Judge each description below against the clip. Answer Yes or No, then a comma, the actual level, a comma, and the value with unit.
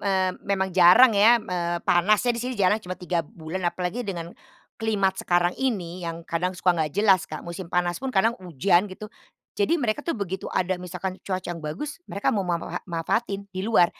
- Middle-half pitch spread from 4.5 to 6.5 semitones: No, average, 2.8 semitones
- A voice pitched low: No, medium, 185 Hz